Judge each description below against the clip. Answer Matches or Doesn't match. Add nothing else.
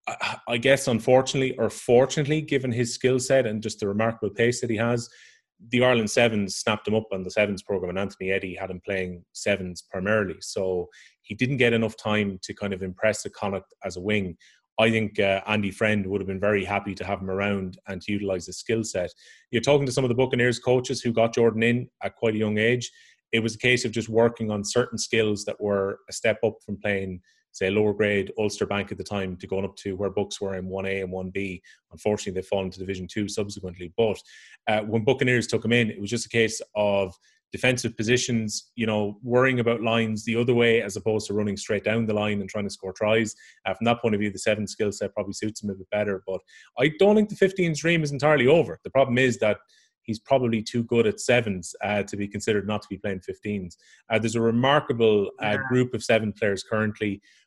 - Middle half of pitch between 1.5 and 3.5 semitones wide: Matches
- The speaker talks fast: Matches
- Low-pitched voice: Matches